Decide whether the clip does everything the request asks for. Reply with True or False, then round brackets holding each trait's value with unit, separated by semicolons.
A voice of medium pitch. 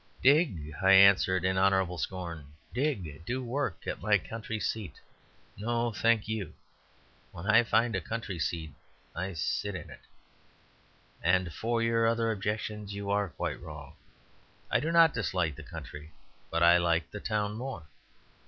False (100 Hz)